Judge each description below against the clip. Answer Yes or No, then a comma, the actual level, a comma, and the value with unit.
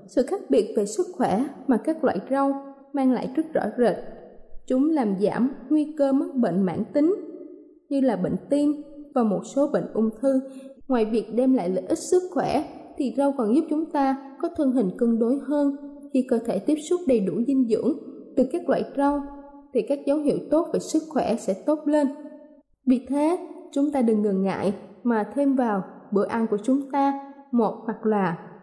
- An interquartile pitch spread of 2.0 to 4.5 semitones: Yes, average, 4.1 semitones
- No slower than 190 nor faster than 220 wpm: Yes, average, 200 wpm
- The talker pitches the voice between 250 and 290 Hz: Yes, very high, 270 Hz